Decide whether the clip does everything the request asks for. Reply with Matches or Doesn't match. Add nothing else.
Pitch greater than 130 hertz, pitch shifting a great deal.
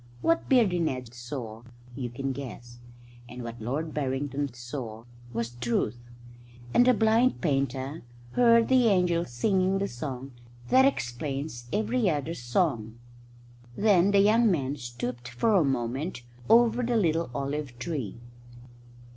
Matches